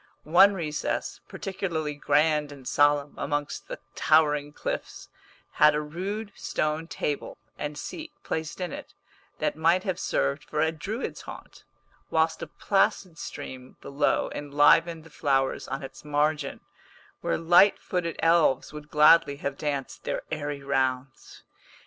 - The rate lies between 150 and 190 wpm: No, slow, 135 wpm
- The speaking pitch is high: No, medium, 150 Hz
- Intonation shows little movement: Yes, narrow, 2.3 semitones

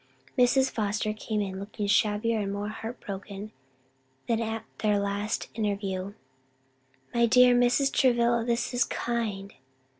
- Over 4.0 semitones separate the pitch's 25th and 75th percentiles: No, average, 2.8 semitones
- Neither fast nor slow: No, slow, 130 wpm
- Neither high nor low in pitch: No, high, 215 Hz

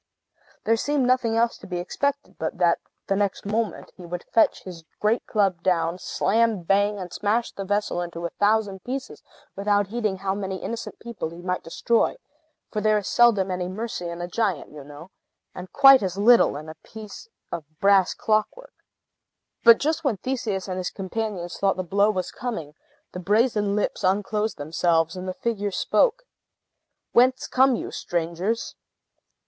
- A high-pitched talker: Yes, high, 200 Hz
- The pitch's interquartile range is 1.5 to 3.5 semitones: No, average, 4.0 semitones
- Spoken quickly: No, average, 170 wpm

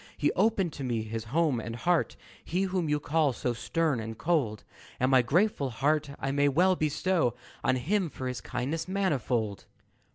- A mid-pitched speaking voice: Yes, medium, 145 Hz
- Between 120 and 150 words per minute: No, average, 175 wpm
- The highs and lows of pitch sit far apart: Yes, wide, 5.7 semitones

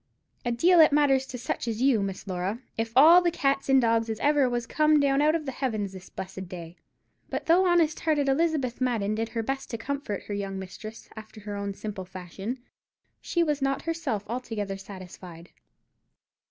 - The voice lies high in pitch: Yes, high, 240 Hz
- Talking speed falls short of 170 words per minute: No, average, 195 wpm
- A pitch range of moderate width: No, wide, 5.9 semitones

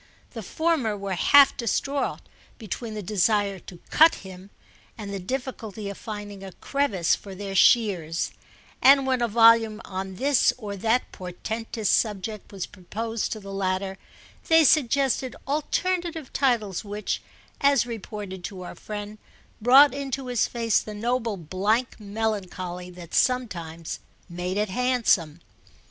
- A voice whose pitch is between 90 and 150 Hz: No, high, 215 Hz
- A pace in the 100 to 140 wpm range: Yes, slow, 135 wpm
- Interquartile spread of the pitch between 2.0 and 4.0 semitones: No, average, 4.6 semitones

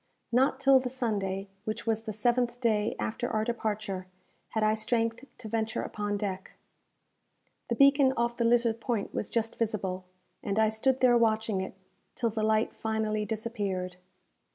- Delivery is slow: No, average, 160 wpm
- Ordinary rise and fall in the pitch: No, narrow, 2.1 semitones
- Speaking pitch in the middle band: No, high, 220 Hz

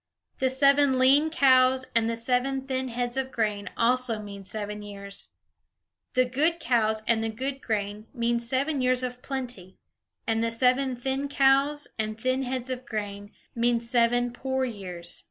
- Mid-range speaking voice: No, high, 245 Hz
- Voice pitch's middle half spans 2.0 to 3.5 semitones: Yes, average, 3.0 semitones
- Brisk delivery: No, average, 160 wpm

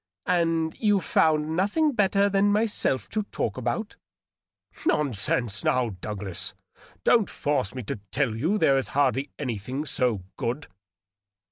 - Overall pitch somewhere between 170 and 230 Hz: No, medium, 145 Hz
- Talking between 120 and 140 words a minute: Yes, slow, 135 wpm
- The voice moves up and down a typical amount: No, wide, 8.3 semitones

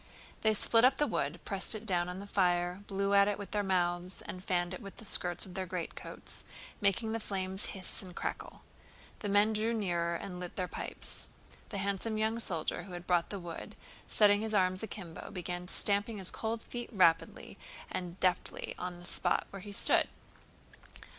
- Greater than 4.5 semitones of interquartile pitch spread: No, average, 2.7 semitones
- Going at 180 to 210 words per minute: Yes, average, 190 wpm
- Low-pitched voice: No, high, 190 Hz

